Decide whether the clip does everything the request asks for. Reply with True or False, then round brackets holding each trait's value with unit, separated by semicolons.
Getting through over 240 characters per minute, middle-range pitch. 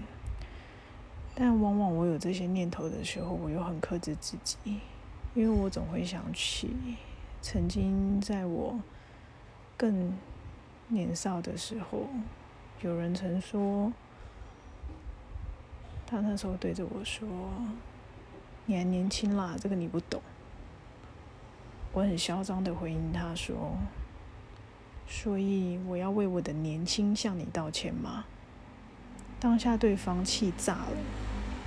False (165 characters per minute; 180 Hz)